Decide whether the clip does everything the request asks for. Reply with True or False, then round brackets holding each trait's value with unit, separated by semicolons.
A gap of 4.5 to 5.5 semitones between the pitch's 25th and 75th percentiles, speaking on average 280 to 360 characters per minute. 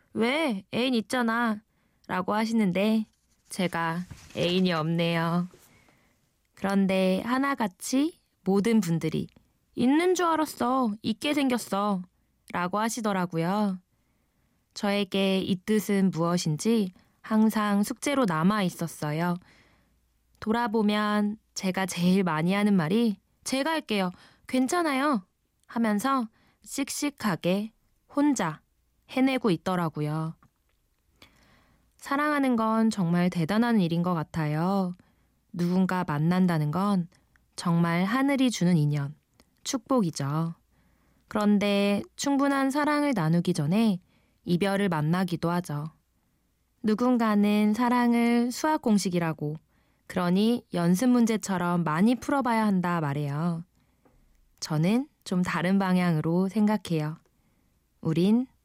False (5.1 semitones; 225 characters per minute)